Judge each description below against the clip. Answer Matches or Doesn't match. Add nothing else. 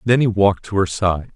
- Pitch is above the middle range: Doesn't match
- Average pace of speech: Doesn't match